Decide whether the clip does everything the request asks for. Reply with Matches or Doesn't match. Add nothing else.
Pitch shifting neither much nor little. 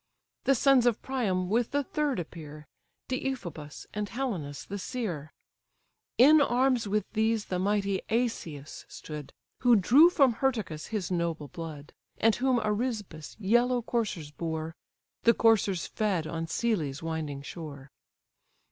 Doesn't match